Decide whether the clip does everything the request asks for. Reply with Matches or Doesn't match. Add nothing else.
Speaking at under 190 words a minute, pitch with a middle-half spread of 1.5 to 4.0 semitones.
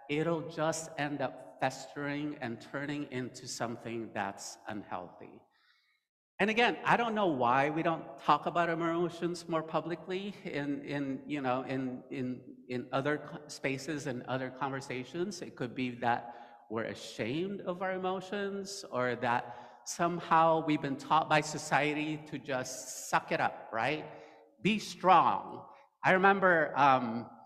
Doesn't match